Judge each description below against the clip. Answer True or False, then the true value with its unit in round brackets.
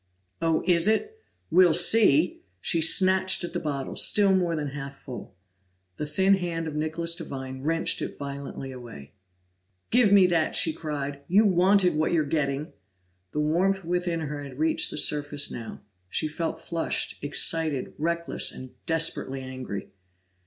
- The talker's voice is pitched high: False (160 Hz)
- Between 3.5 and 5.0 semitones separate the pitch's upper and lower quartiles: True (3.8 semitones)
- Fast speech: False (150 wpm)